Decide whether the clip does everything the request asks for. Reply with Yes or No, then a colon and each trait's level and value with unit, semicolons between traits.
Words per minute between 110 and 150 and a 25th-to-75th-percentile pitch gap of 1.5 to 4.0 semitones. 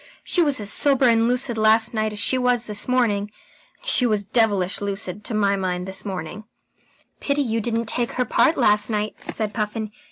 No: average, 195 wpm; average, 2.9 semitones